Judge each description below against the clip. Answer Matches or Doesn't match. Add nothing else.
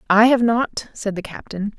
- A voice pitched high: Matches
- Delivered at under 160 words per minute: Doesn't match